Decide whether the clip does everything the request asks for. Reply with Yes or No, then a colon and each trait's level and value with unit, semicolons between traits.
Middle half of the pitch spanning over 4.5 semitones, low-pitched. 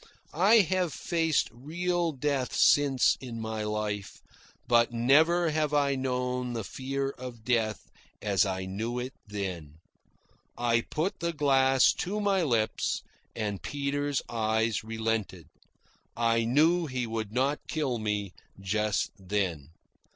Yes: average, 5.0 semitones; low, 125 Hz